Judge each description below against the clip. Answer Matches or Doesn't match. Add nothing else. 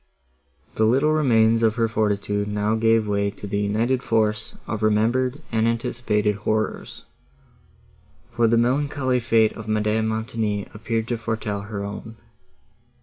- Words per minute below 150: Matches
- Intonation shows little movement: Matches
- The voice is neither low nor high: Doesn't match